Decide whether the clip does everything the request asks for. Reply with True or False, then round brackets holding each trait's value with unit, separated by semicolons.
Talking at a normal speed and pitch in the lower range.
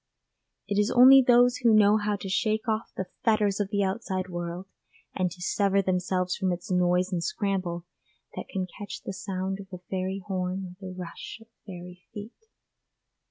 False (180 wpm; 190 Hz)